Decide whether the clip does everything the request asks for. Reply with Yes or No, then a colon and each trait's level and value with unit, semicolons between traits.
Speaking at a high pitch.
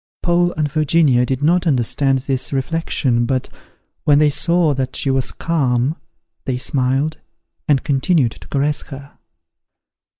No: medium, 140 Hz